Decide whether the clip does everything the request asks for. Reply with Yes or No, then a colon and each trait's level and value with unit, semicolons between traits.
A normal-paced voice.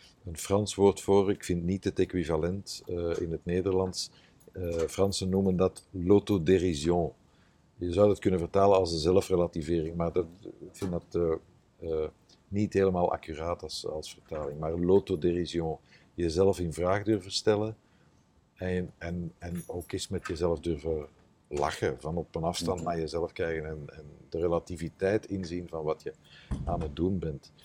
Yes: average, 160 wpm